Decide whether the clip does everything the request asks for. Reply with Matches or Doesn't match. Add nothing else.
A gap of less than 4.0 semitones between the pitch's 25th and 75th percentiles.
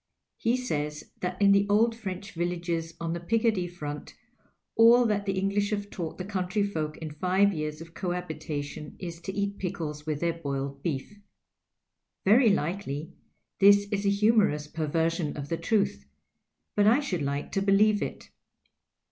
Doesn't match